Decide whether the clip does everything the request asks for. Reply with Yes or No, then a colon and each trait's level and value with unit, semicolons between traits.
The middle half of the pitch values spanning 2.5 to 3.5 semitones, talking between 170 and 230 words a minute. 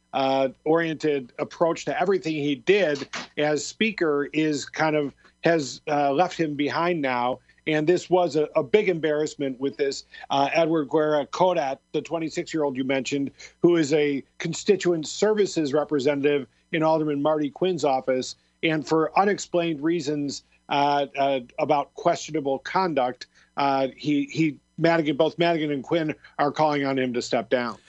No: average, 2.8 semitones; average, 155 wpm